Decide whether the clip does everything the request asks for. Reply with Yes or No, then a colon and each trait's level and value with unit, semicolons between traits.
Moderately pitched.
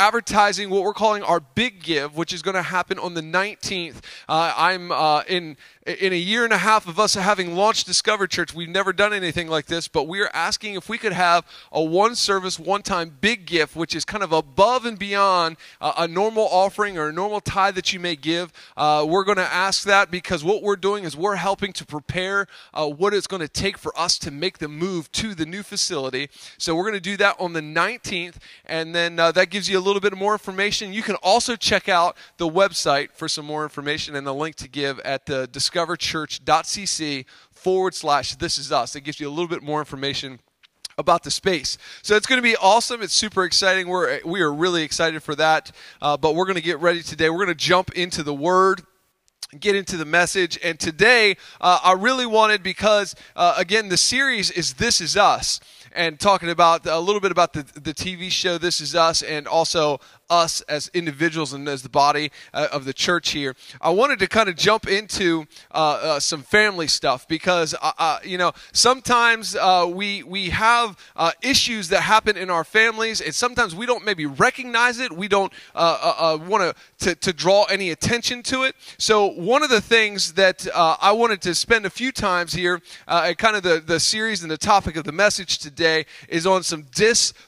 Yes: medium, 180 Hz